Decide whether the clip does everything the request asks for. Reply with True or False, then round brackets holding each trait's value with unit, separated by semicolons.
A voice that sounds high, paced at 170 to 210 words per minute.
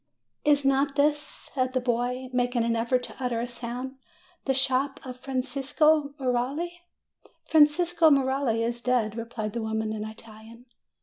False (255 Hz; 145 wpm)